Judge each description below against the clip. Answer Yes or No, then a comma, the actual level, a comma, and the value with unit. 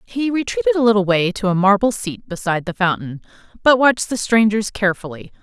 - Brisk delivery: No, average, 190 wpm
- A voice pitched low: No, high, 210 Hz